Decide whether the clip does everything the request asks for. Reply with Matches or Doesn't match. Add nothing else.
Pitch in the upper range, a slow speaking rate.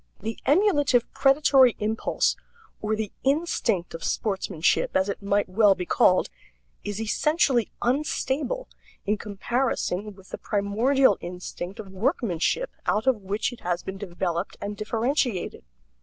Matches